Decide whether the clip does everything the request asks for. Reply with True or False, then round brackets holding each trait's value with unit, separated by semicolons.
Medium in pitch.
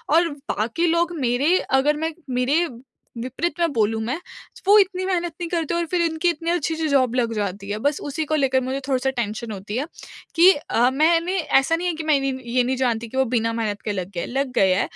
False (275 Hz)